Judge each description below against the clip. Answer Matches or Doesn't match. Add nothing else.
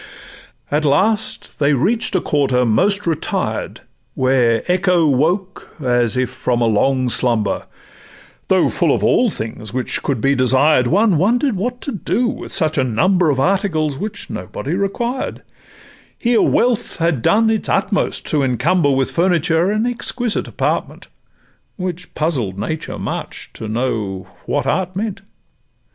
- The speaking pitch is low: Doesn't match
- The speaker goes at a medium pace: Matches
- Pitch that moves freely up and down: Matches